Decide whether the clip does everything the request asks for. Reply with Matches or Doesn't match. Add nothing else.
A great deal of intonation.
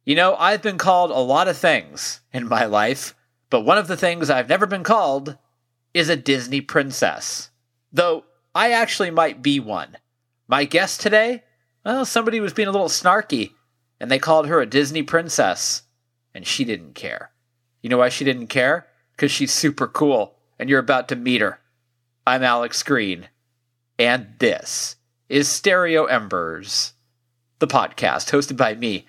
Matches